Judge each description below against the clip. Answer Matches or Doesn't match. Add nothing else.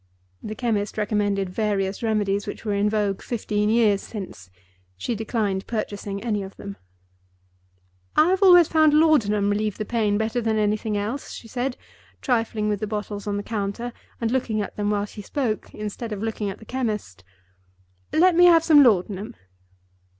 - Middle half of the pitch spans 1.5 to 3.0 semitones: Matches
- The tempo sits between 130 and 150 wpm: Doesn't match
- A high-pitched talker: Matches